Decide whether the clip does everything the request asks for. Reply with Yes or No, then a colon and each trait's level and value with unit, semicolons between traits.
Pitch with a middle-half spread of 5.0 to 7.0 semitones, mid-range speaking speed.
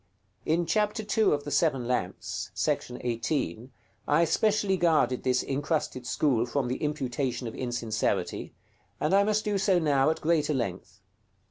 Yes: wide, 5.5 semitones; average, 150 wpm